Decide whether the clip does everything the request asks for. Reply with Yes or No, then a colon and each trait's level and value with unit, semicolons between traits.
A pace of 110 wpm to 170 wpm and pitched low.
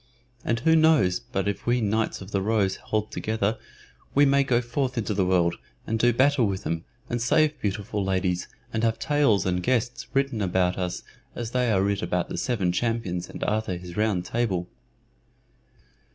No: average, 185 wpm; low, 110 Hz